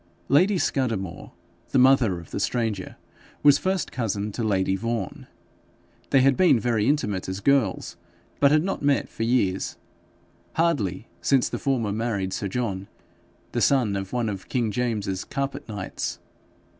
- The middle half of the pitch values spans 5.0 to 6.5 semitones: Yes, wide, 5.6 semitones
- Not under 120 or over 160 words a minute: Yes, average, 150 wpm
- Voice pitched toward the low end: Yes, low, 115 Hz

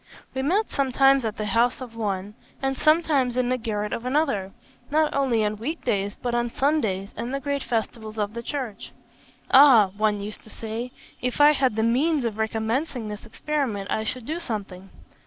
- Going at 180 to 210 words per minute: Yes, average, 190 wpm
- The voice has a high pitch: Yes, high, 235 Hz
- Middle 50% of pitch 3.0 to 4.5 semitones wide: Yes, average, 4.2 semitones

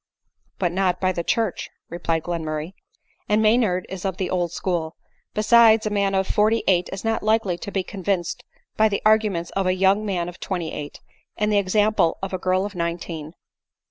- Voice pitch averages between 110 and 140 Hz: No, high, 190 Hz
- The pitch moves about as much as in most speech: Yes, average, 3.3 semitones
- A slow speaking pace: No, average, 200 wpm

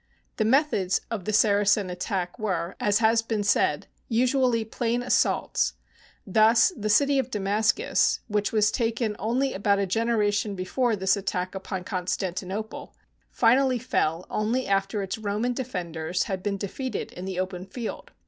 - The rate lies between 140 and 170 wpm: Yes, average, 155 wpm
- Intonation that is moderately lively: Yes, average, 3.3 semitones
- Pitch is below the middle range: No, high, 210 Hz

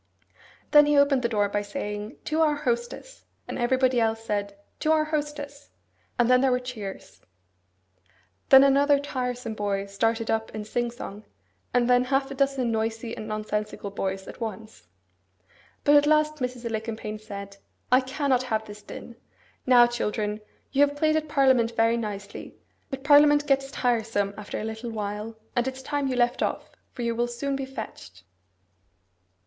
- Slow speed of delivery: No, average, 165 wpm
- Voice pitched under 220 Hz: No, high, 240 Hz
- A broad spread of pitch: No, average, 4.2 semitones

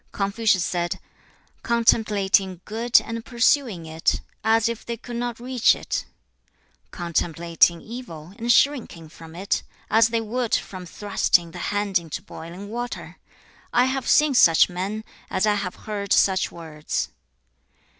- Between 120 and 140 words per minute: Yes, slow, 135 wpm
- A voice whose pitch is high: Yes, high, 205 Hz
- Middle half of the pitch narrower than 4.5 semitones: No, average, 5.1 semitones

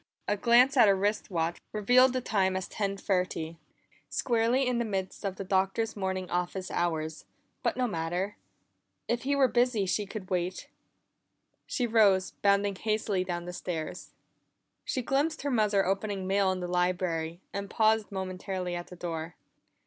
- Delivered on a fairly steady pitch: No, average, 3.5 semitones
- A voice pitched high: Yes, high, 195 Hz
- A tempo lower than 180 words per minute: Yes, average, 165 wpm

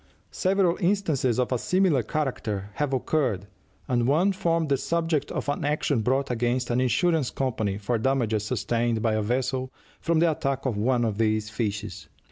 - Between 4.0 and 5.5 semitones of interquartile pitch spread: Yes, average, 5.2 semitones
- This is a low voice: Yes, low, 130 Hz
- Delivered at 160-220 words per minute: Yes, average, 170 wpm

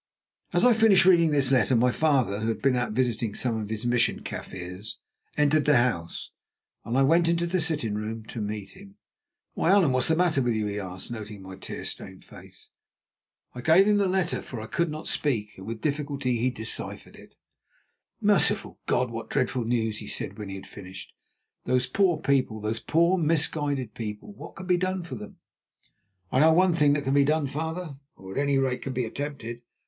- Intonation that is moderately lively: No, wide, 6.3 semitones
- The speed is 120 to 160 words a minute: No, fast, 205 wpm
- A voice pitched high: No, low, 130 Hz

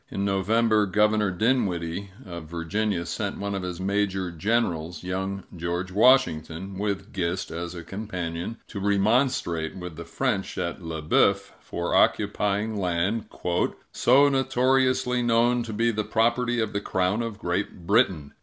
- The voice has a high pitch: No, low, 100 Hz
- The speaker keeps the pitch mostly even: No, average, 4.5 semitones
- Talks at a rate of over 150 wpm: No, average, 145 wpm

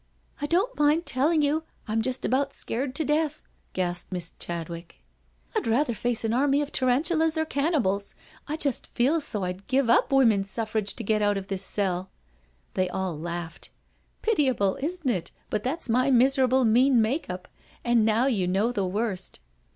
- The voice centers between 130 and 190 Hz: No, high, 240 Hz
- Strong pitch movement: Yes, wide, 6.3 semitones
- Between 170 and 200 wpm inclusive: Yes, average, 185 wpm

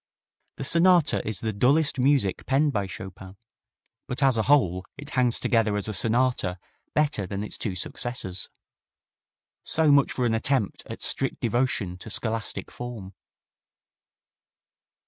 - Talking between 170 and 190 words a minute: No, average, 140 wpm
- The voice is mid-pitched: No, low, 120 Hz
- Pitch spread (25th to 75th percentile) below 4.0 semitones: No, average, 5.3 semitones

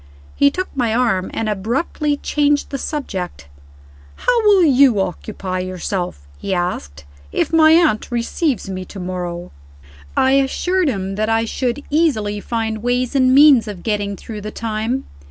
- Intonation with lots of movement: Yes, wide, 6.4 semitones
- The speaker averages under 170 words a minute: Yes, average, 155 wpm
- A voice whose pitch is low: No, high, 225 Hz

